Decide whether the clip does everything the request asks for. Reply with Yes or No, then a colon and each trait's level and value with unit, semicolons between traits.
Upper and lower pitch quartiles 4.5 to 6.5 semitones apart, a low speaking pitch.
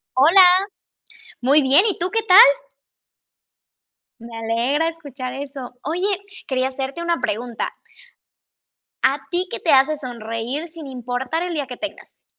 No: average, 4.8 semitones; very high, 275 Hz